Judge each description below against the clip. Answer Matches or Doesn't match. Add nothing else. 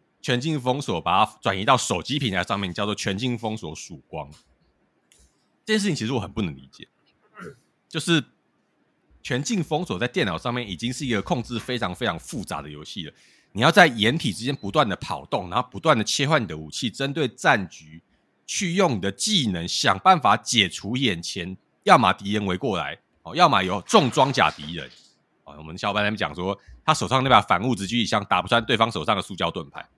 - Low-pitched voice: Matches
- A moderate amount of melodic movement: Doesn't match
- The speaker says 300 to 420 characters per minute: Matches